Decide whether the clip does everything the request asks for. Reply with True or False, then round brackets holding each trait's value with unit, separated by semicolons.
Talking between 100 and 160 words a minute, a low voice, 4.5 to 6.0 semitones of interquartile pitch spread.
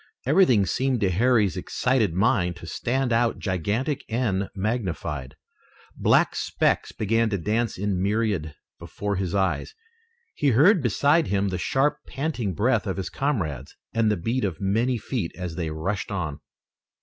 True (150 wpm; 105 Hz; 5.1 semitones)